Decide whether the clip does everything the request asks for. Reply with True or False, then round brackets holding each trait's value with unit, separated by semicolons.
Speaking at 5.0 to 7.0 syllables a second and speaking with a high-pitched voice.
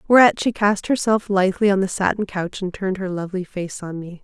True (5.9 syllables/s; 195 Hz)